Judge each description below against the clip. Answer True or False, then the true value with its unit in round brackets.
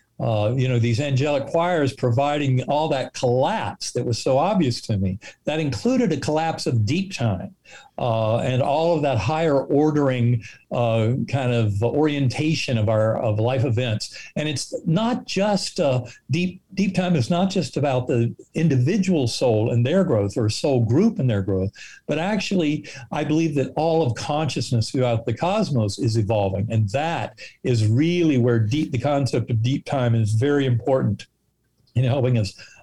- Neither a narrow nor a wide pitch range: True (4.9 semitones)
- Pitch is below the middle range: True (130 Hz)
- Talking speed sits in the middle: True (170 wpm)